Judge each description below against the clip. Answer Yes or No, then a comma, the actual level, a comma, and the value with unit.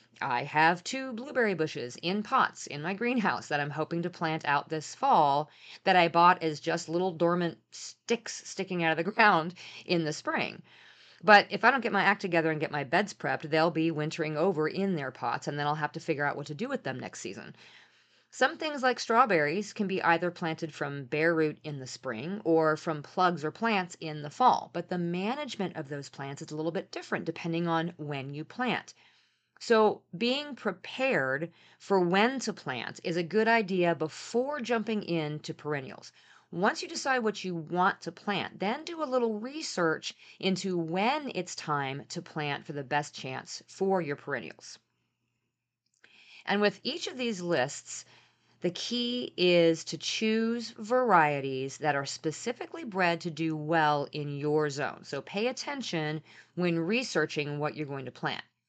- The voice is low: No, medium, 170 Hz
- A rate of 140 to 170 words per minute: No, average, 185 wpm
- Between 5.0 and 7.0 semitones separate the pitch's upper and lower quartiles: Yes, wide, 5.4 semitones